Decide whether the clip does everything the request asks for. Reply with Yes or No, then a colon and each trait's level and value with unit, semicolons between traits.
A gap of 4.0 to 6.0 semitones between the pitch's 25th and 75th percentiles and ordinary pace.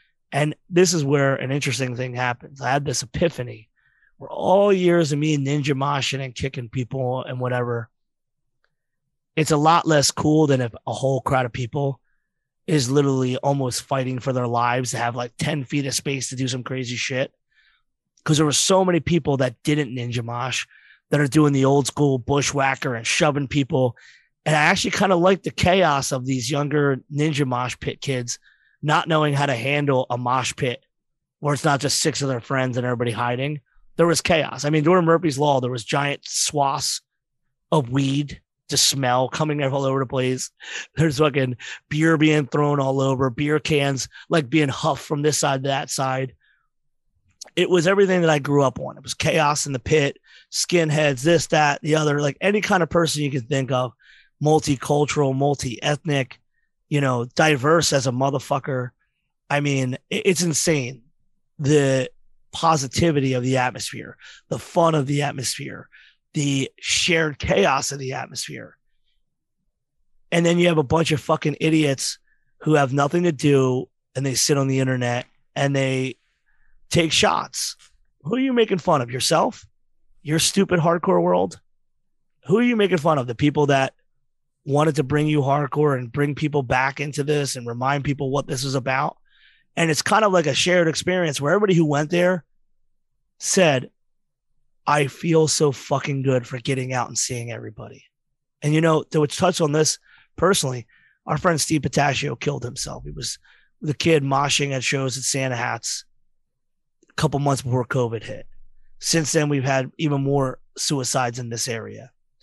No: average, 2.9 semitones; average, 175 wpm